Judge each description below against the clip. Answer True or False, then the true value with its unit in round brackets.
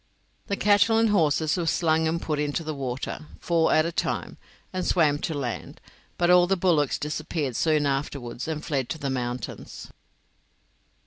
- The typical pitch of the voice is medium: True (155 Hz)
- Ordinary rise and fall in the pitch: True (3.3 semitones)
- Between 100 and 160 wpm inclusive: False (170 wpm)